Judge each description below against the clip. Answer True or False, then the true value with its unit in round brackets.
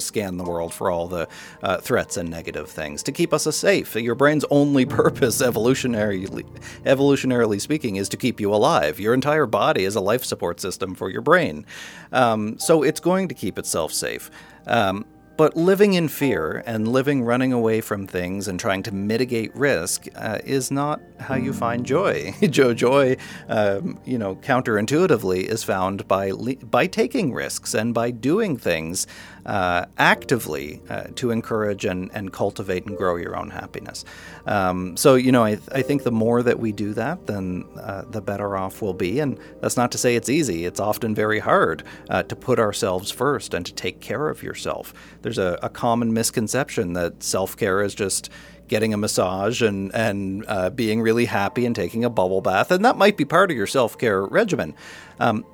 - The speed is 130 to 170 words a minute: False (190 wpm)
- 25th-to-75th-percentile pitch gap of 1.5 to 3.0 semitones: False (4.8 semitones)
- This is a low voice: True (110 Hz)